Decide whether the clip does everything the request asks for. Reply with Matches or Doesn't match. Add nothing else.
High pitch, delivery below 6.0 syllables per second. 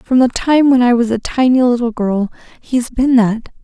Matches